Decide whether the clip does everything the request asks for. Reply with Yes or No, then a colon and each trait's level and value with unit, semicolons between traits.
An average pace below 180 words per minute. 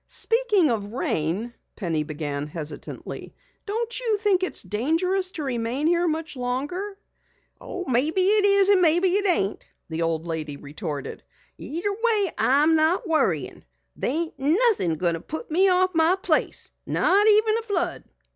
Yes: average, 145 wpm